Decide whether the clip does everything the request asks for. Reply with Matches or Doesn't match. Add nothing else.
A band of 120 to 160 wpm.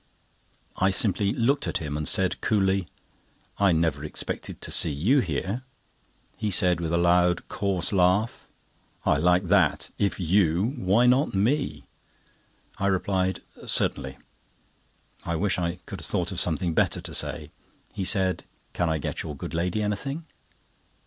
Matches